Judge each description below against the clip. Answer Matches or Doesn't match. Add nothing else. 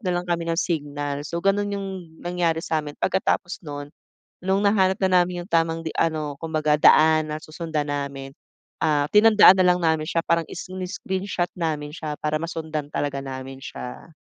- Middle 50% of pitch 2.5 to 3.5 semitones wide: Matches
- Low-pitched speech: Doesn't match